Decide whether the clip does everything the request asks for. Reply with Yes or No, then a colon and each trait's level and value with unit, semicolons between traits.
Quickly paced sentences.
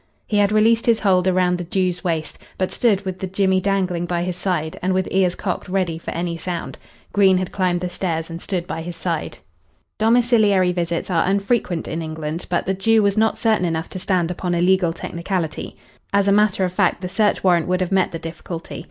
Yes: fast, 215 wpm